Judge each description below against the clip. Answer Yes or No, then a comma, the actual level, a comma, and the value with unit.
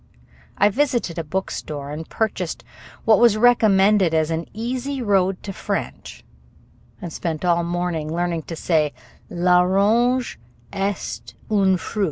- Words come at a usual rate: No, slow, 130 wpm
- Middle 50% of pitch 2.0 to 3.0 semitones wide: No, average, 4.4 semitones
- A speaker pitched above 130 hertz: Yes, medium, 185 Hz